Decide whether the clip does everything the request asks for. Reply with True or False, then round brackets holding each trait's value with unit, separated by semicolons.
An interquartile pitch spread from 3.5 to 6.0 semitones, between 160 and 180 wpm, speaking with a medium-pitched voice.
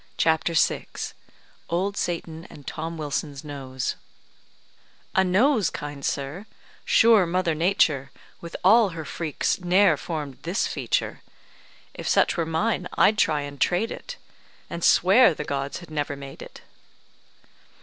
False (4.1 semitones; 135 wpm; 165 Hz)